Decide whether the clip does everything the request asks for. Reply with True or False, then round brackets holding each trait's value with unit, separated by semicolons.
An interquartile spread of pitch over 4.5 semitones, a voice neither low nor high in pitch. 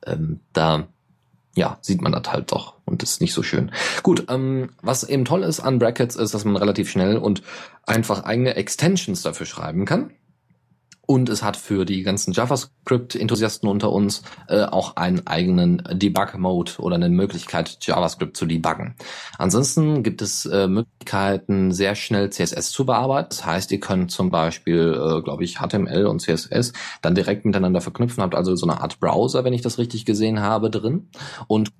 False (5.0 semitones; 110 Hz)